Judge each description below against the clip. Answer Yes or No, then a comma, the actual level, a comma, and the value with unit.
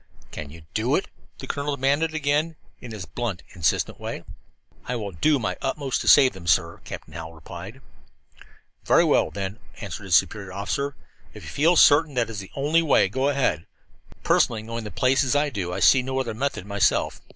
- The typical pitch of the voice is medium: No, low, 120 Hz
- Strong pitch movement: Yes, wide, 6.6 semitones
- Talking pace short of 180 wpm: No, average, 195 wpm